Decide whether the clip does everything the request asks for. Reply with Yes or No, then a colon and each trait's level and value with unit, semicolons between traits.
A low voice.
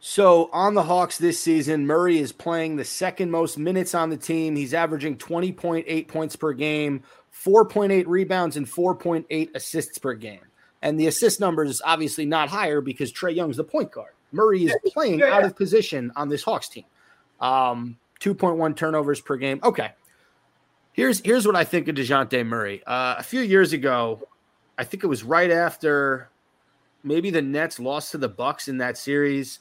No: medium, 160 Hz